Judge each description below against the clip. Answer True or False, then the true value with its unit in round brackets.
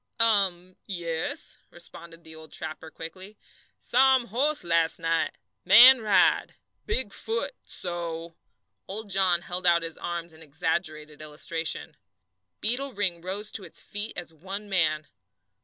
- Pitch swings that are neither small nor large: True (4.0 semitones)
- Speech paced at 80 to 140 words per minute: True (135 wpm)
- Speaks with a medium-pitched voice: True (175 Hz)